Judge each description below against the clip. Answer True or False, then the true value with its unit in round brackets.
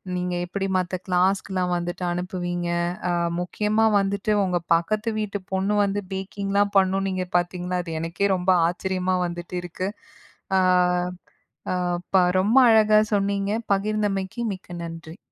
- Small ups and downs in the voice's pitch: True (2.1 semitones)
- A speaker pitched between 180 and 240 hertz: True (190 Hz)